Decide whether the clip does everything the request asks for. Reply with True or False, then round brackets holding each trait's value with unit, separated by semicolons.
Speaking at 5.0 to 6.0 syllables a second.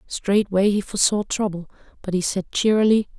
True (5.4 syllables/s)